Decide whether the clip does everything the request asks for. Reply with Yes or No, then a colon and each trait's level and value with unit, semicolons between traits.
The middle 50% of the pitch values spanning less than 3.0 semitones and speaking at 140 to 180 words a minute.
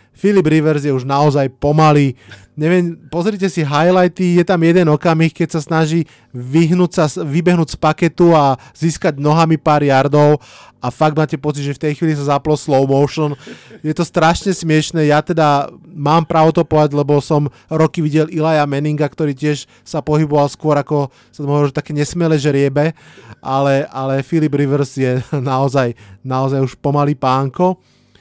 Yes: narrow, 2.5 semitones; fast, 165 wpm